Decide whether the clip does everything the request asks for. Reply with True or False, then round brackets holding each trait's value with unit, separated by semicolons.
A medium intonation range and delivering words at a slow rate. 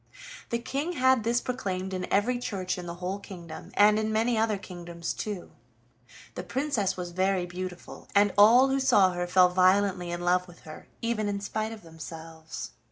False (3.7 semitones; 180 wpm)